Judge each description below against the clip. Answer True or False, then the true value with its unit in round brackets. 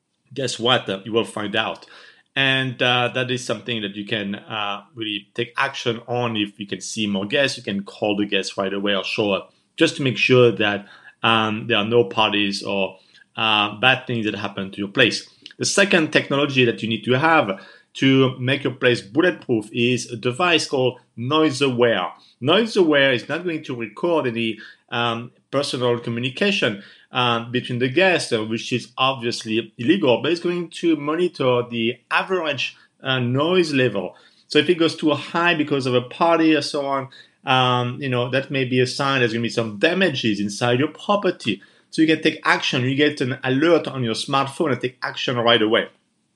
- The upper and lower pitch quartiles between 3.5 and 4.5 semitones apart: True (3.9 semitones)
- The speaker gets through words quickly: False (190 wpm)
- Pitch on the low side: True (125 Hz)